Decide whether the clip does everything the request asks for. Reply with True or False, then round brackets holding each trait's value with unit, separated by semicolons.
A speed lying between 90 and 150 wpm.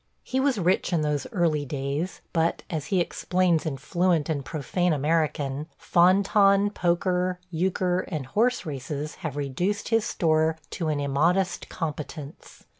True (145 wpm)